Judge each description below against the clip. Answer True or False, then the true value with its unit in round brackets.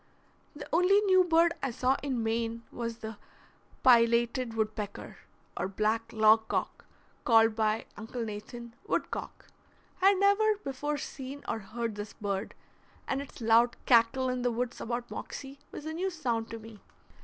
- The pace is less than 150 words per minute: False (160 wpm)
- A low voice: False (235 Hz)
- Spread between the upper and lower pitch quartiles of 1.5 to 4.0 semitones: True (3.6 semitones)